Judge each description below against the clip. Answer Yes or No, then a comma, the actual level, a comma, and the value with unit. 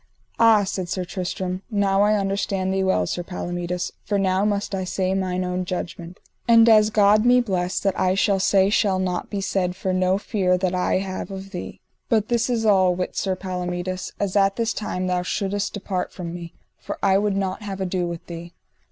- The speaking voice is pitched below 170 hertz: No, high, 190 Hz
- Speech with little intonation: Yes, narrow, 1.8 semitones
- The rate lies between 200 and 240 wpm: Yes, fast, 205 wpm